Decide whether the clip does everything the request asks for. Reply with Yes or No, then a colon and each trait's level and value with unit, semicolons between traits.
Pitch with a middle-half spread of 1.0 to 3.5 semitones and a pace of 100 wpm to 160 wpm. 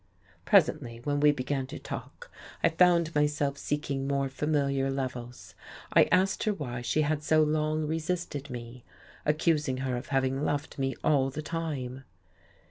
Yes: narrow, 2.6 semitones; average, 150 wpm